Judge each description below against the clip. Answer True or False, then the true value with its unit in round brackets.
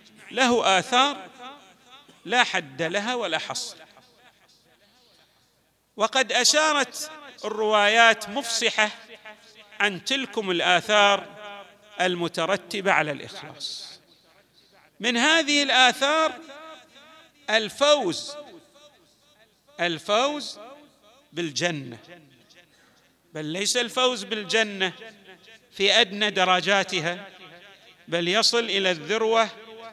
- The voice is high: True (220 Hz)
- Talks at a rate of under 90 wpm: True (70 wpm)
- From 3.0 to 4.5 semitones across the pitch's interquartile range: False (5.3 semitones)